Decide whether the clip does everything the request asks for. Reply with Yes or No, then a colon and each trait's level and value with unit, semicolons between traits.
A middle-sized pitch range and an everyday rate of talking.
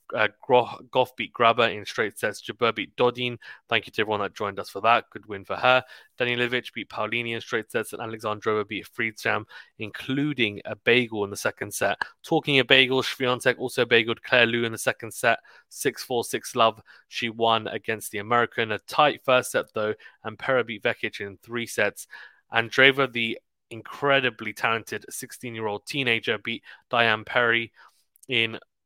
No: narrow, 2.1 semitones; average, 180 wpm